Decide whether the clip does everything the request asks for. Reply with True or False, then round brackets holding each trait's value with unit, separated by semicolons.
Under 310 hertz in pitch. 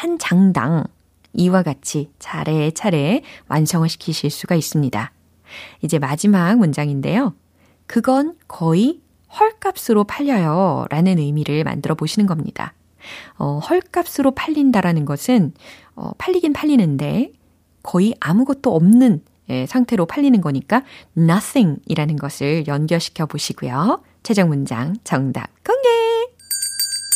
True (190 Hz)